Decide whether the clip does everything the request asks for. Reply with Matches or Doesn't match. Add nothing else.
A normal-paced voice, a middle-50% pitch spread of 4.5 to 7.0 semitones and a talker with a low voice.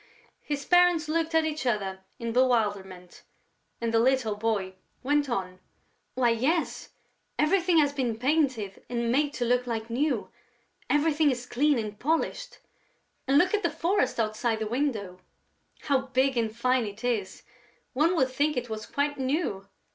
Doesn't match